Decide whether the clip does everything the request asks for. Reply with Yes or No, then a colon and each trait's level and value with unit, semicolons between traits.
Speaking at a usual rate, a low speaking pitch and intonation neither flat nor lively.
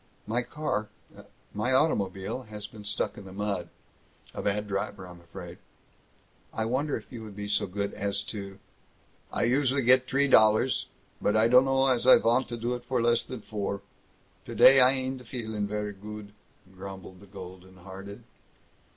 Yes: average, 170 wpm; low, 105 Hz; average, 4.0 semitones